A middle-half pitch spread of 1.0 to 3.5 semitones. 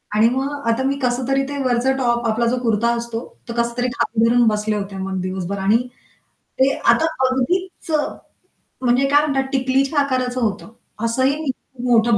Yes: average, 2.8 semitones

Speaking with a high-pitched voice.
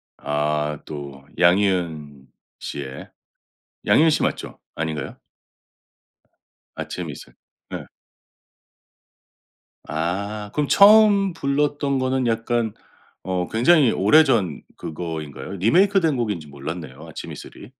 No: low, 100 Hz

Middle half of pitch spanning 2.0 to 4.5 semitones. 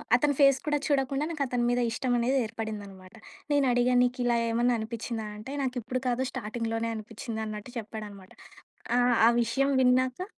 Yes: average, 2.8 semitones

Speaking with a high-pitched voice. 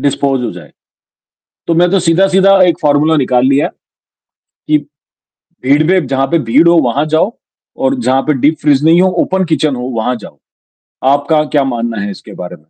No: medium, 145 Hz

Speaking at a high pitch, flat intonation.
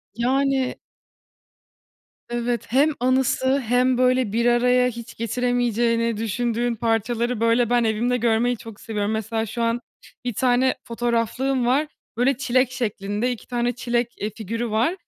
Yes: high, 240 Hz; narrow, 1.5 semitones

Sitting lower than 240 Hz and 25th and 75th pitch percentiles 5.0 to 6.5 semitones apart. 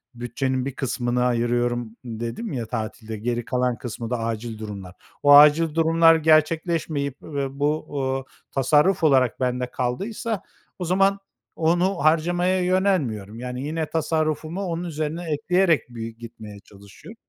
Yes: medium, 140 Hz; wide, 5.4 semitones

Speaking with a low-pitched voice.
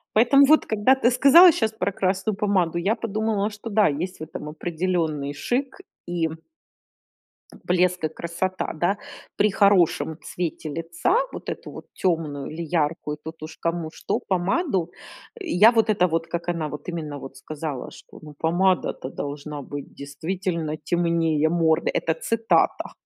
No: medium, 175 Hz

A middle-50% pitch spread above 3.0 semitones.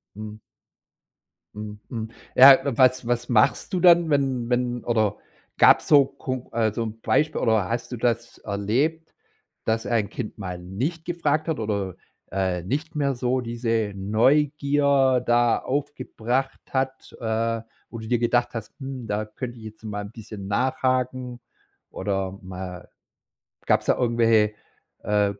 Yes: average, 3.6 semitones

